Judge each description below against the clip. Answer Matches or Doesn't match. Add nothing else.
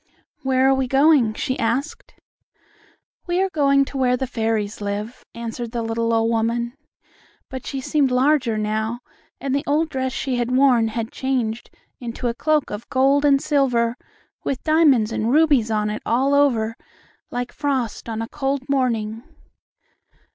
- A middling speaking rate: Matches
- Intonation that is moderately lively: Matches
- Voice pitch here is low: Doesn't match